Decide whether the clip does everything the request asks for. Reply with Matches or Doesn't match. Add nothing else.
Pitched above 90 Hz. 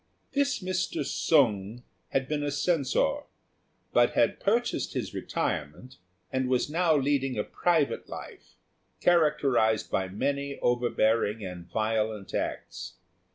Matches